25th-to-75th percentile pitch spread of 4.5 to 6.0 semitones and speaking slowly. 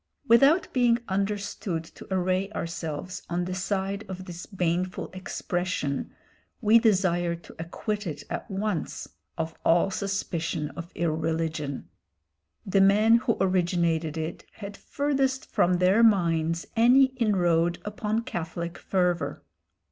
No: average, 3.6 semitones; slow, 120 wpm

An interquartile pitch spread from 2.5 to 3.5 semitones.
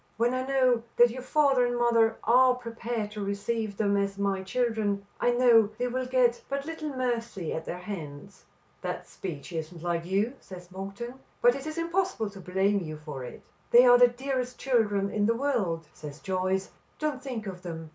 No: average, 4.7 semitones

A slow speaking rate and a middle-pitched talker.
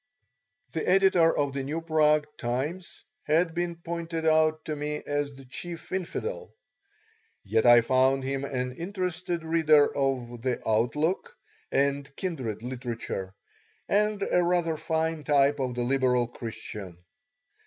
Yes: slow, 130 wpm; medium, 150 Hz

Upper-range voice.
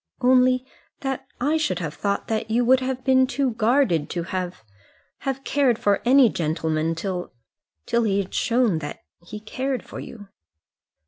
Yes: high, 235 Hz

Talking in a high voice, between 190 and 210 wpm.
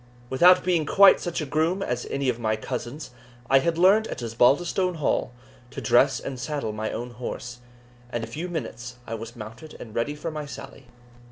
No: low, 135 Hz; average, 195 wpm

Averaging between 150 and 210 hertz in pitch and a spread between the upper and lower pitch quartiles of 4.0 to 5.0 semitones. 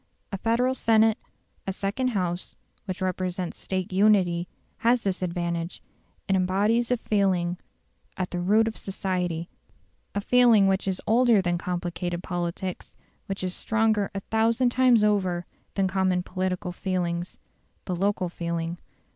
No: high, 190 Hz; average, 3.2 semitones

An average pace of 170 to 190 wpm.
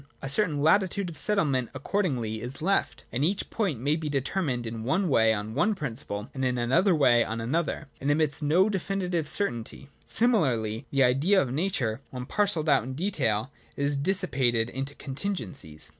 Yes: average, 175 wpm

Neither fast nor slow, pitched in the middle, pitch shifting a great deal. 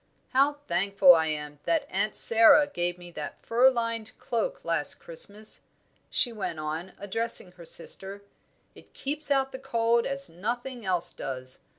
No: average, 155 wpm; high, 220 Hz; wide, 7.0 semitones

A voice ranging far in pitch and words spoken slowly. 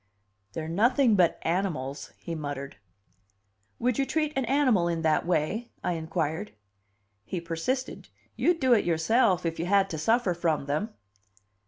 No: wide, 6.4 semitones; average, 150 wpm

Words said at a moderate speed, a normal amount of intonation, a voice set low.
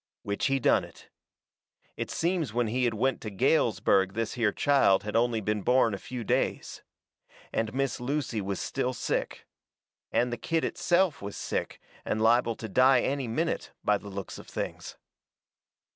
Yes: average, 170 wpm; average, 4.0 semitones; low, 120 Hz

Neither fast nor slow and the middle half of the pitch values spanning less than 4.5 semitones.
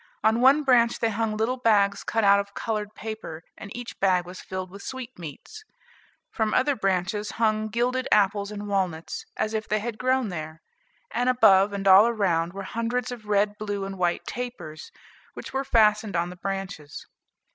Yes: average, 180 wpm; average, 3.2 semitones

